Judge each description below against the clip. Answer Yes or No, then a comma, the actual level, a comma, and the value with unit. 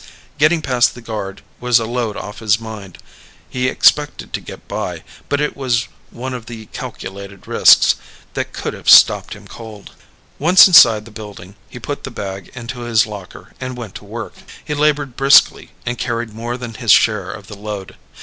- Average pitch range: Yes, average, 3.4 semitones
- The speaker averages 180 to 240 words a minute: Yes, average, 185 wpm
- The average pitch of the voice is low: Yes, low, 115 Hz